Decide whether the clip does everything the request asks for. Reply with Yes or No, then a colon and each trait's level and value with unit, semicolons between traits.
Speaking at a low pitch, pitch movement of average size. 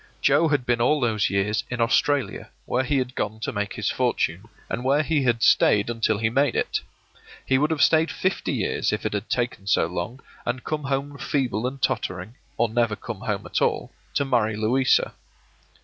Yes: low, 120 Hz; average, 4.3 semitones